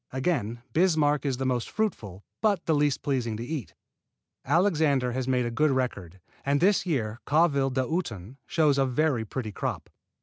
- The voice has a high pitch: No, low, 135 Hz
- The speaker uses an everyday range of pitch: Yes, average, 4.5 semitones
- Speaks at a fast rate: No, average, 165 wpm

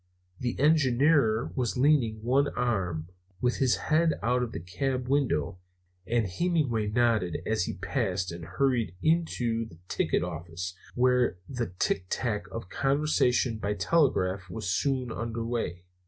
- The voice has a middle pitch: No, low, 115 Hz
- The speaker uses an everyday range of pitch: No, wide, 5.9 semitones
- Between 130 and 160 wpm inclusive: Yes, average, 145 wpm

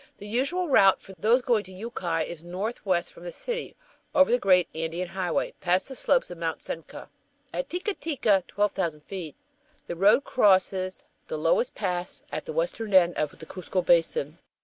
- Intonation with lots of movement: Yes, wide, 5.8 semitones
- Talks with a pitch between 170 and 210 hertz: Yes, high, 190 Hz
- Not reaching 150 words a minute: No, average, 175 wpm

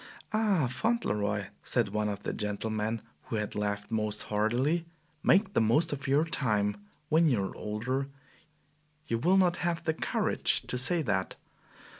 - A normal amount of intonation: No, wide, 7.4 semitones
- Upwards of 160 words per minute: No, average, 155 wpm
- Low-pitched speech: Yes, low, 120 Hz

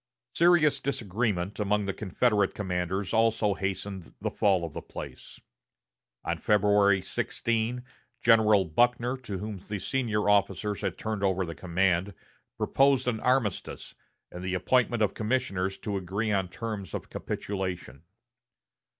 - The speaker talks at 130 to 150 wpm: Yes, slow, 135 wpm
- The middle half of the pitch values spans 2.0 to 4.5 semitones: Yes, average, 3.2 semitones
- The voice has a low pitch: Yes, low, 105 Hz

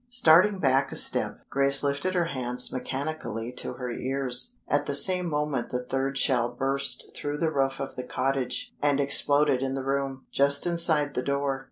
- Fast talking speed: No, average, 180 wpm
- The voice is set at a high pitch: No, medium, 140 Hz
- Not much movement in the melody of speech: Yes, narrow, 1.9 semitones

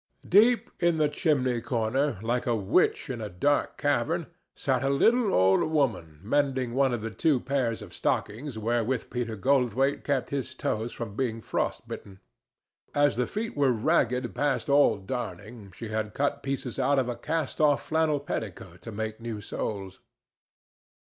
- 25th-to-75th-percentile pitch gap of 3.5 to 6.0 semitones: Yes, average, 4.5 semitones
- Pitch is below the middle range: Yes, low, 125 Hz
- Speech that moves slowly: No, average, 165 wpm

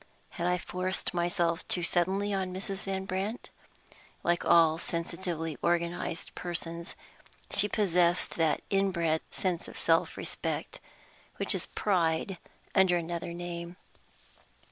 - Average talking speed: No, slow, 120 wpm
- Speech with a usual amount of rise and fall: No, narrow, 2.0 semitones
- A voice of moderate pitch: Yes, medium, 175 Hz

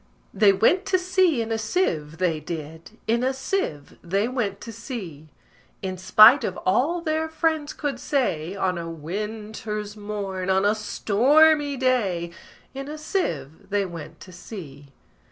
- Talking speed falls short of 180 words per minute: Yes, average, 155 wpm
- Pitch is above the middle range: Yes, high, 210 Hz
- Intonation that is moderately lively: No, wide, 6.9 semitones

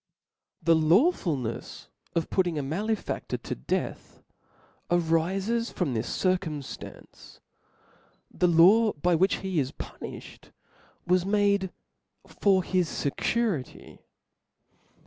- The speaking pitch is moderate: Yes, medium, 180 Hz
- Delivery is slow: Yes, slow, 100 wpm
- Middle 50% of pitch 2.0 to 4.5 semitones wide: Yes, average, 3.9 semitones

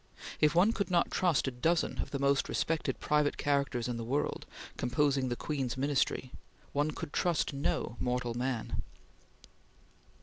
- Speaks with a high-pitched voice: No, medium, 140 Hz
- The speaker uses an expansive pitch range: No, average, 3.3 semitones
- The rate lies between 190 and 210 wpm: No, average, 155 wpm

